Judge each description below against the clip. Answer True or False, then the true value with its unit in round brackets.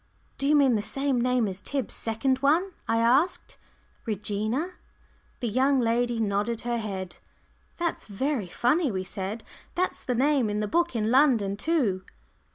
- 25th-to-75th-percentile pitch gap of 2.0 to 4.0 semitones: False (4.7 semitones)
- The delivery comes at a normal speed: True (160 wpm)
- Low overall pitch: False (240 Hz)